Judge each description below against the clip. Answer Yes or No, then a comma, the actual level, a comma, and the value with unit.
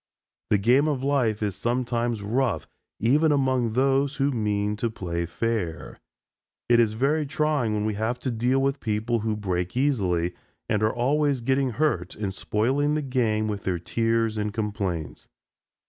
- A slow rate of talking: No, average, 160 wpm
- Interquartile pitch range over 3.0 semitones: Yes, average, 4.2 semitones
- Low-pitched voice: Yes, low, 115 Hz